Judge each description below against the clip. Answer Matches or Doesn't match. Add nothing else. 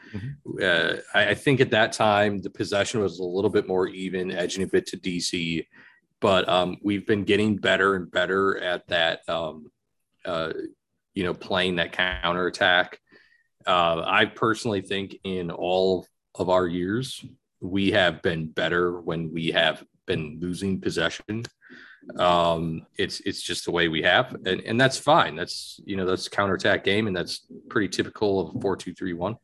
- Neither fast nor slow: Matches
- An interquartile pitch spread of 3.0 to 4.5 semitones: Doesn't match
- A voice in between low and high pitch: Doesn't match